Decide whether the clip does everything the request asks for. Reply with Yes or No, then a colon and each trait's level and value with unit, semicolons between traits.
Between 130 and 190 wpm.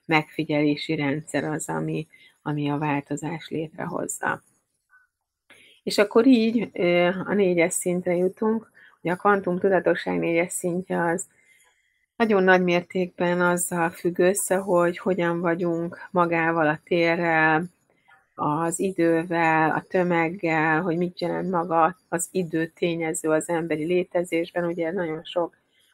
No: average, 120 wpm